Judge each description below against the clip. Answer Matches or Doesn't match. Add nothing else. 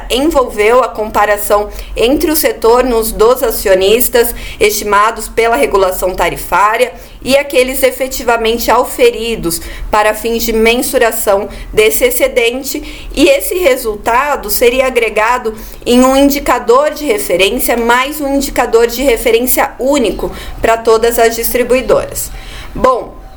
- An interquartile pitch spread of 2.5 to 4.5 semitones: Doesn't match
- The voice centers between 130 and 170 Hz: Doesn't match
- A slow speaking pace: Matches